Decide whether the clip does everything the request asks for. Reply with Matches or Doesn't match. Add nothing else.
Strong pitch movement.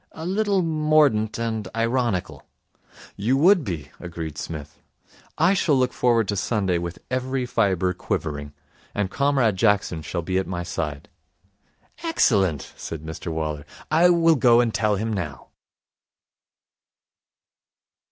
Matches